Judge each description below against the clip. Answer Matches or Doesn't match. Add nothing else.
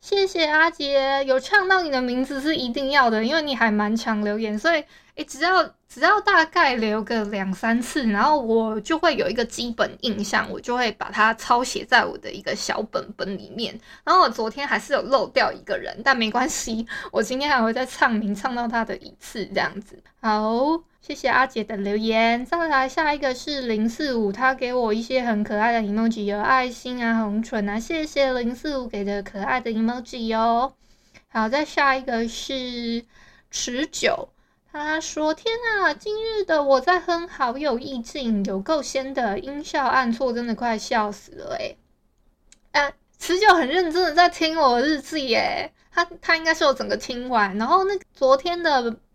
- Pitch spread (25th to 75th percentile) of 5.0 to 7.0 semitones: Matches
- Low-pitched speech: Doesn't match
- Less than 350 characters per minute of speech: Matches